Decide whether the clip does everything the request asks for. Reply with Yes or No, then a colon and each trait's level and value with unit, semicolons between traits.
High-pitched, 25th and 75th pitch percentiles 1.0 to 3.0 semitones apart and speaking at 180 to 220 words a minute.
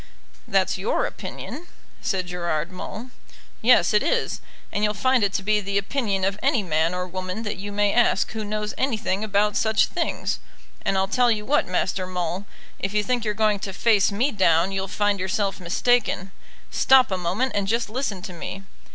Yes: high, 205 Hz; average, 2.7 semitones; average, 190 wpm